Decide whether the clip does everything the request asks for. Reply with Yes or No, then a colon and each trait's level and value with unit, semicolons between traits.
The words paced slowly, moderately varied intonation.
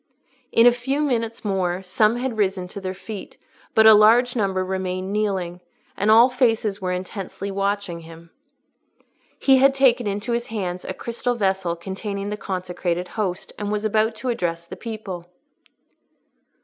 No: average, 160 wpm; average, 3.6 semitones